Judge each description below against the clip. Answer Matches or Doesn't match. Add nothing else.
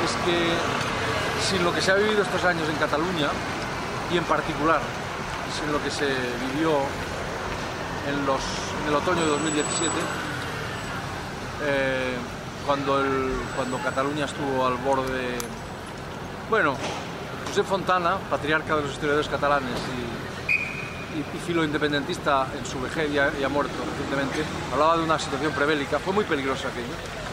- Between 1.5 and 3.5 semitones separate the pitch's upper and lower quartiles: Matches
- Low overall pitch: Doesn't match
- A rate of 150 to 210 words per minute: Doesn't match